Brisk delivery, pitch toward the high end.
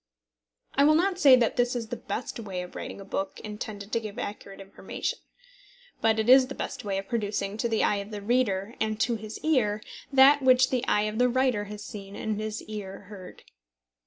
Yes: fast, 215 wpm; high, 215 Hz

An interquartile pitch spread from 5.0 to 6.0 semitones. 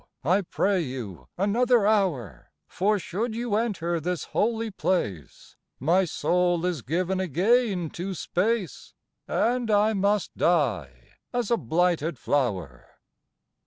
Yes: wide, 5.6 semitones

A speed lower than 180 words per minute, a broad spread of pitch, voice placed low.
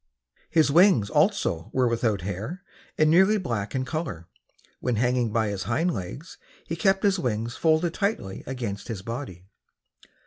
Yes: average, 150 wpm; wide, 7.9 semitones; low, 125 Hz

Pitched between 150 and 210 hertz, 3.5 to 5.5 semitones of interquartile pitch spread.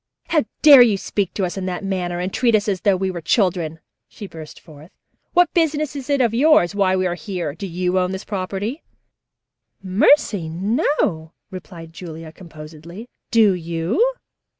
Yes: high, 190 Hz; average, 5.0 semitones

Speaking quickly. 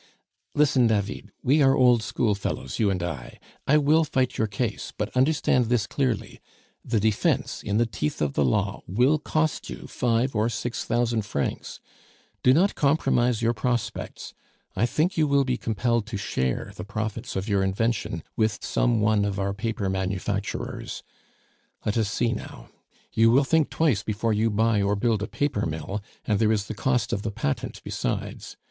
No: average, 175 wpm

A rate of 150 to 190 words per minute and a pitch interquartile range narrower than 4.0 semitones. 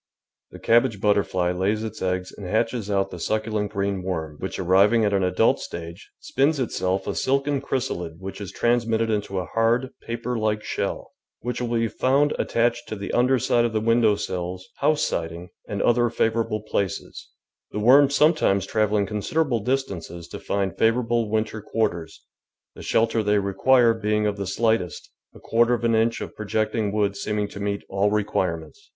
Yes: average, 175 wpm; average, 3.3 semitones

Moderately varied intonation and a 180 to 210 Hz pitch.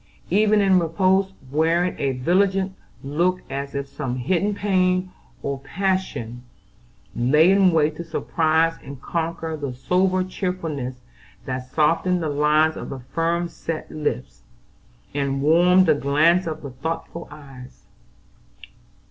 No: average, 4.6 semitones; medium, 160 Hz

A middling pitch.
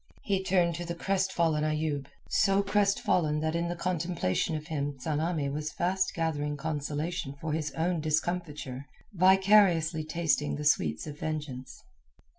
Yes: medium, 160 Hz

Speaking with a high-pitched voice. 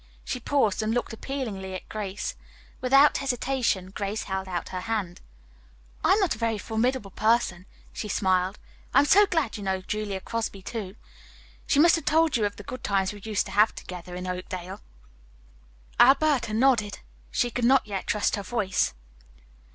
Yes: high, 215 Hz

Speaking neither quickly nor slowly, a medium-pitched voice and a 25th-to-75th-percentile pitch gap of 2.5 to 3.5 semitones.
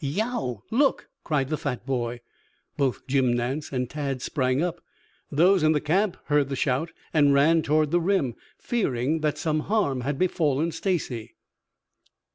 No: average, 155 wpm; medium, 150 Hz; average, 4.0 semitones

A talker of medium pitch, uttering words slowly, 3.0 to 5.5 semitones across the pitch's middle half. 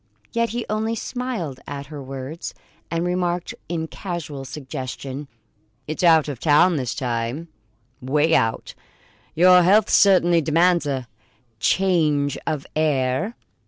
Yes: medium, 160 Hz; slow, 125 wpm; average, 4.4 semitones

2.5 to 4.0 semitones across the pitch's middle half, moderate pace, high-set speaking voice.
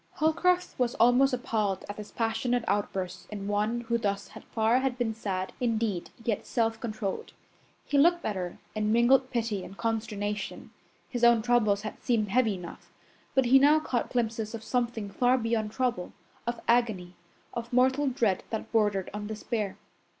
Yes: average, 2.9 semitones; average, 165 wpm; high, 225 Hz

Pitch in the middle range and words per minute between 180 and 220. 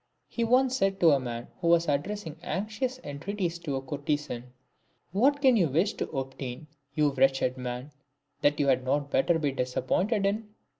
Yes: medium, 155 Hz; average, 185 wpm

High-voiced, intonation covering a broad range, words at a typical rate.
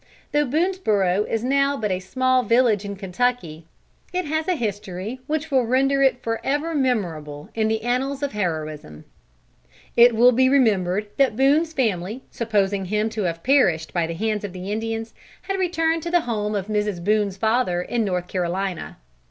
Yes: high, 220 Hz; wide, 5.8 semitones; average, 170 wpm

